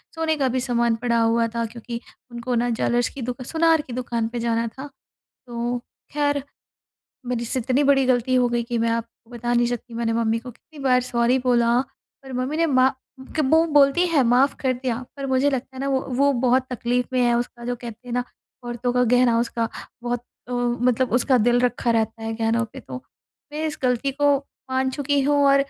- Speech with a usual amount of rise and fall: No, narrow, 1.9 semitones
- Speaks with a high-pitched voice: Yes, high, 245 Hz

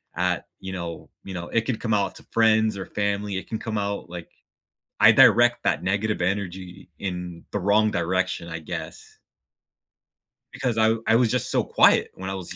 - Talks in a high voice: No, low, 100 Hz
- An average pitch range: Yes, average, 3.4 semitones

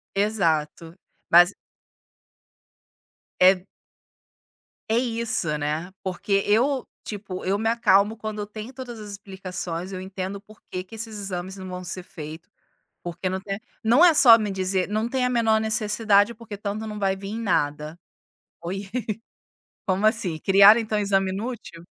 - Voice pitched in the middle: No, high, 200 Hz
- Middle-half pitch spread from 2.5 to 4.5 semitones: Yes, average, 2.9 semitones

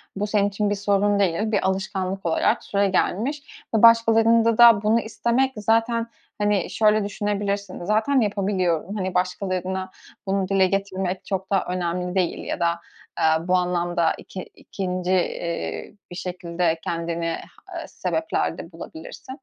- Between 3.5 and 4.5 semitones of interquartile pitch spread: No, average, 2.7 semitones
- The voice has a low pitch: No, high, 195 Hz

